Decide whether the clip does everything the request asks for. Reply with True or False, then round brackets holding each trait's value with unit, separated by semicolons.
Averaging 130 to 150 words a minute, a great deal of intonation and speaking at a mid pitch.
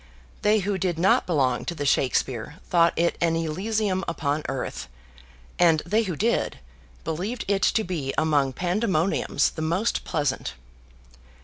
False (140 wpm; 4.6 semitones; 170 Hz)